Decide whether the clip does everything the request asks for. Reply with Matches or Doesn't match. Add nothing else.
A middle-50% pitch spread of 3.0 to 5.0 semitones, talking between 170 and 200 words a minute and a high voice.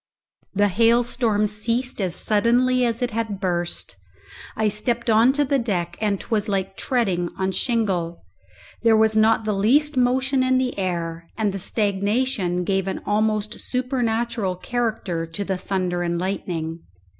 Doesn't match